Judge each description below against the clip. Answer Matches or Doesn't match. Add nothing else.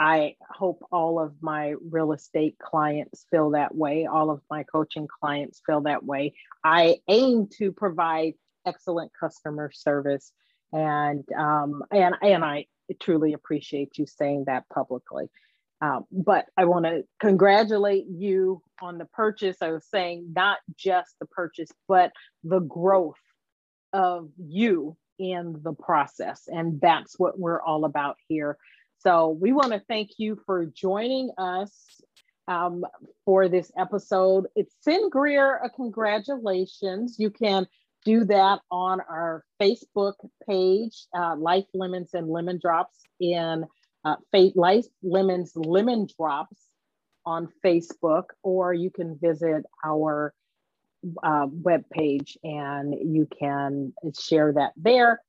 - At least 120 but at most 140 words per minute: Matches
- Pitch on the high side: Doesn't match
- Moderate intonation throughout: Matches